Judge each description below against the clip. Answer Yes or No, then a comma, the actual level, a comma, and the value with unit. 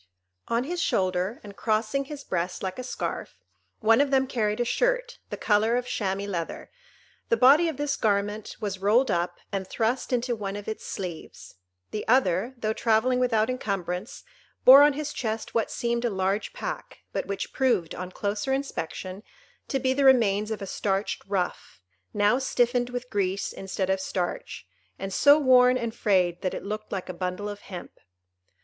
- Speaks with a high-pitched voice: Yes, high, 215 Hz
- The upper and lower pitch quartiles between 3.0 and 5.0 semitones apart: Yes, average, 4.6 semitones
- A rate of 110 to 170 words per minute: No, average, 180 wpm